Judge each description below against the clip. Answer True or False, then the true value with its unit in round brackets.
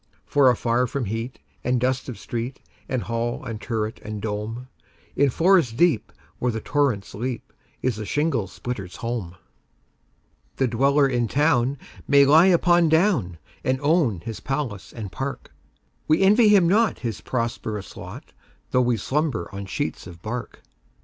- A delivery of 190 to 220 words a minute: False (135 wpm)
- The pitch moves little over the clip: False (4.7 semitones)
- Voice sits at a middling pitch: False (125 Hz)